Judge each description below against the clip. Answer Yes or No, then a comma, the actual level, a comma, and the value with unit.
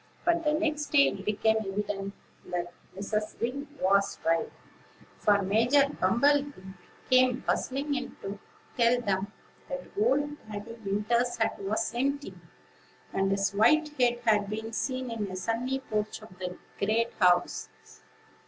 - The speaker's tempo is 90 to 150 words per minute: Yes, average, 145 wpm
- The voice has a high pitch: Yes, high, 225 Hz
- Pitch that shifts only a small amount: No, average, 5.1 semitones